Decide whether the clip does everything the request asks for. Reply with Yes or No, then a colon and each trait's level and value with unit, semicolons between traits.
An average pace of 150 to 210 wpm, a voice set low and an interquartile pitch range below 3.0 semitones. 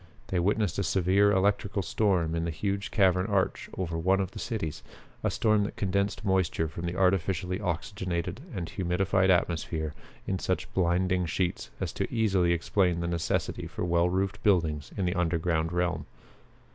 Yes: average, 165 wpm; very low, 90 Hz; narrow, 2.4 semitones